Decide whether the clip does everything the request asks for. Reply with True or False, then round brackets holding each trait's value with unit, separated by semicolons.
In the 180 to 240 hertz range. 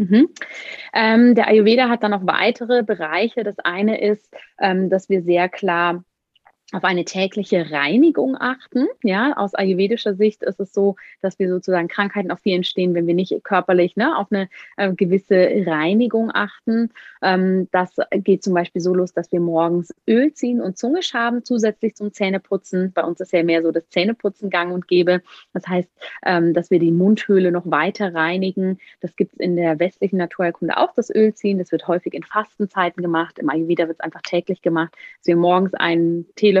True (190 Hz)